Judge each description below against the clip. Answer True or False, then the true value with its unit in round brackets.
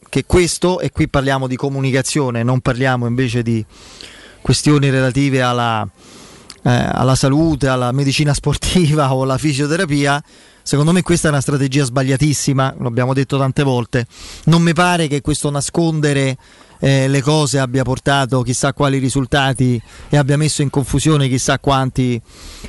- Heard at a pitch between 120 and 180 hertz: True (140 Hz)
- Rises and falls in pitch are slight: True (2.2 semitones)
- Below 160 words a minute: True (145 wpm)